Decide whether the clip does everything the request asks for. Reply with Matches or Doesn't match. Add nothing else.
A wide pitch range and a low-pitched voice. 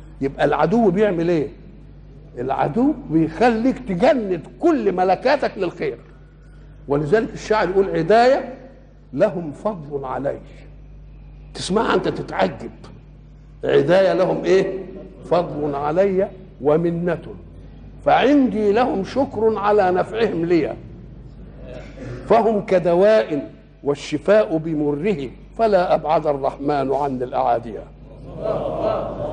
Doesn't match